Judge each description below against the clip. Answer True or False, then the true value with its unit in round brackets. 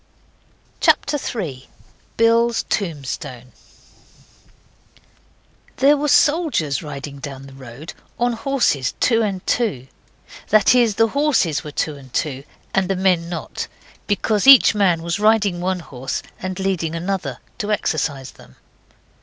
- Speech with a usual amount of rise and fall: False (7.9 semitones)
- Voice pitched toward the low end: False (185 Hz)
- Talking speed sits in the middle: False (130 wpm)